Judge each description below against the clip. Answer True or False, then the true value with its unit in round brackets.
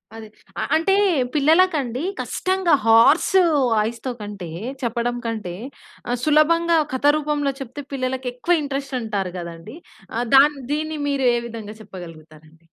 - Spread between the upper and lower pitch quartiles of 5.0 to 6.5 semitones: True (5.5 semitones)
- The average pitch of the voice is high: True (255 Hz)